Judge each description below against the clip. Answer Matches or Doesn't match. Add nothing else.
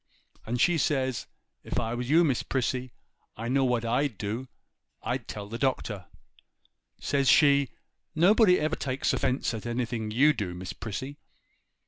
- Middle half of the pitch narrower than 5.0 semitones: Matches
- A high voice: Doesn't match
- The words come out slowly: Doesn't match